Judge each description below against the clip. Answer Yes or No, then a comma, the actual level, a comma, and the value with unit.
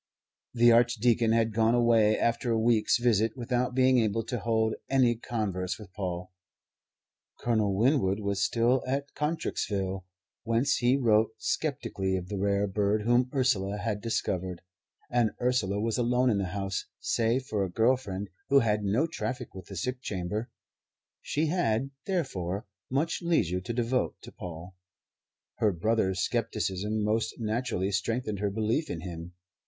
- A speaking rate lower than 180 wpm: Yes, average, 150 wpm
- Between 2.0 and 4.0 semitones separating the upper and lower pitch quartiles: Yes, average, 3.7 semitones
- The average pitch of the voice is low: Yes, low, 110 Hz